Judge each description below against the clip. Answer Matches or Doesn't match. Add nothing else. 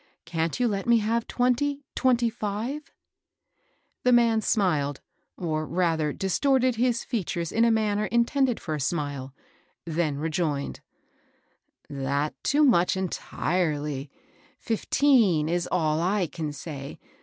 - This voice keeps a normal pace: Doesn't match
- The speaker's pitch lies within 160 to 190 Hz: Matches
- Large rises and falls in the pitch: Matches